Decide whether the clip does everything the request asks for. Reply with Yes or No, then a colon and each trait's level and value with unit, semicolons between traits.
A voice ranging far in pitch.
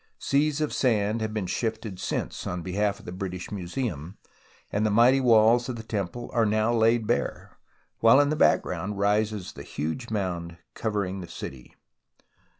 No: average, 3.8 semitones